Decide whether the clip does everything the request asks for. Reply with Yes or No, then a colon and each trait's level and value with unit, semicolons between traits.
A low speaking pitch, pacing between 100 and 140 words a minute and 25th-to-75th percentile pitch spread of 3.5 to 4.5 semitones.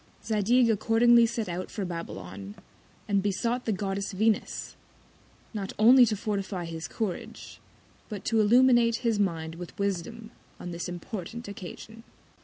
No: high, 205 Hz; slow, 135 wpm; average, 4.2 semitones